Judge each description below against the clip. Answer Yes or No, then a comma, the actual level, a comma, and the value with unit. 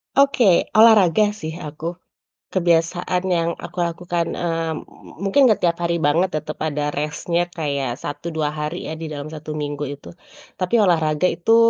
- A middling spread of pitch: Yes, average, 3.0 semitones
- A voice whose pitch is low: No, medium, 165 Hz